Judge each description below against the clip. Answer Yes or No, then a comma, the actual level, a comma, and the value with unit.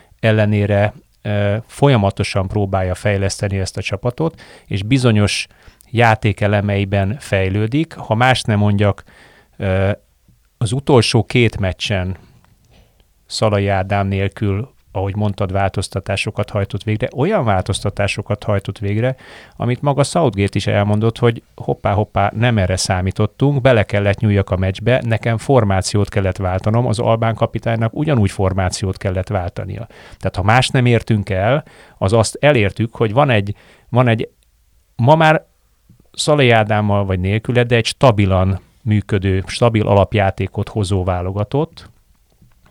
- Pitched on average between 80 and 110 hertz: Yes, low, 105 Hz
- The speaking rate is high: No, average, 120 wpm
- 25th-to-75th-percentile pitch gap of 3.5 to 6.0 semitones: No, average, 3.0 semitones